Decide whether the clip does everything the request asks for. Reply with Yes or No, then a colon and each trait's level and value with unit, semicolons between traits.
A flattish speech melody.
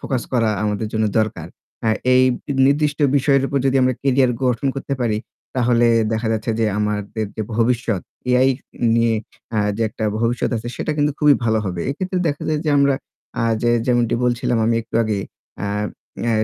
No: average, 3.6 semitones